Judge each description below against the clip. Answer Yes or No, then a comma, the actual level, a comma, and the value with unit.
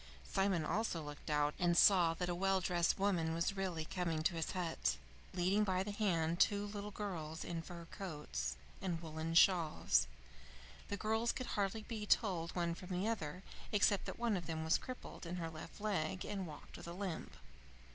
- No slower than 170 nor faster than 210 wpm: Yes, average, 185 wpm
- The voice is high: No, medium, 180 Hz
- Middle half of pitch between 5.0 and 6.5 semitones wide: No, average, 3.5 semitones